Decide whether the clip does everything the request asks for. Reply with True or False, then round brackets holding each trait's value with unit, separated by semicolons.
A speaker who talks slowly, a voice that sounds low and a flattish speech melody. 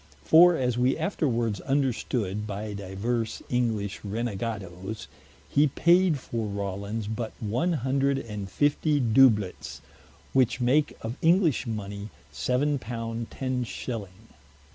False (115 wpm; 115 Hz; 4.4 semitones)